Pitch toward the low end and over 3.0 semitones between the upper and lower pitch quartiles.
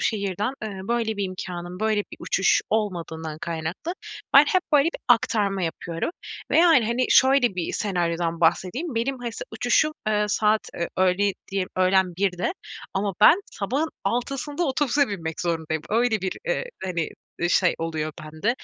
No: high, 200 Hz; wide, 5.5 semitones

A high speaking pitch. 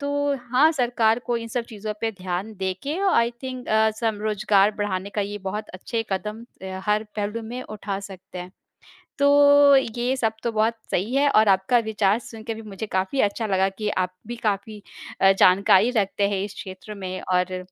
Yes: high, 210 Hz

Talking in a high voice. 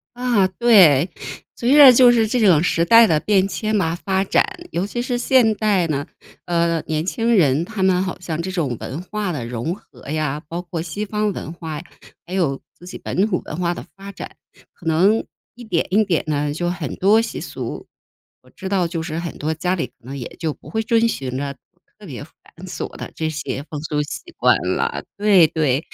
No: medium, 180 Hz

